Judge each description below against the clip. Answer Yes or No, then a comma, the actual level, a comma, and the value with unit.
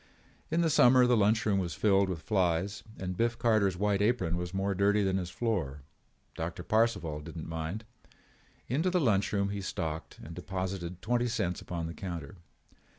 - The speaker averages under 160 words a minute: No, average, 180 wpm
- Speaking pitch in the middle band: No, very low, 95 Hz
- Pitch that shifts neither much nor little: Yes, average, 4.0 semitones